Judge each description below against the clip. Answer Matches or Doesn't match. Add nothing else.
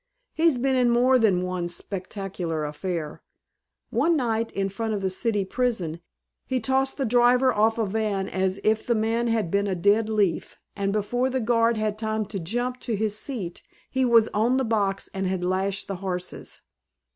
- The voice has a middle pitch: Doesn't match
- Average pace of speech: Matches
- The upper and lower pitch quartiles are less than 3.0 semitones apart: Doesn't match